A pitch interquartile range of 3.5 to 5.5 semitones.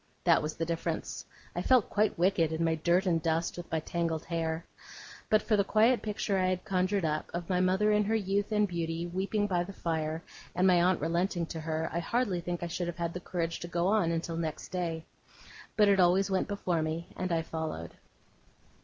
No: average, 2.8 semitones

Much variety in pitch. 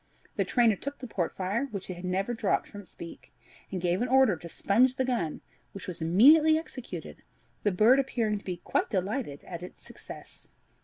Yes: wide, 5.8 semitones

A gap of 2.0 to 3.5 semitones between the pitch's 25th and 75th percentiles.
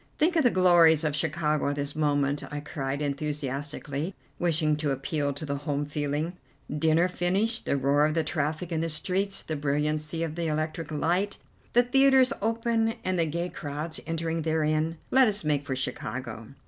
Yes: average, 3.2 semitones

